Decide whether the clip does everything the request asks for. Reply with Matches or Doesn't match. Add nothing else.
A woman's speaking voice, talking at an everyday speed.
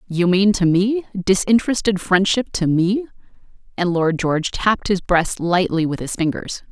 Matches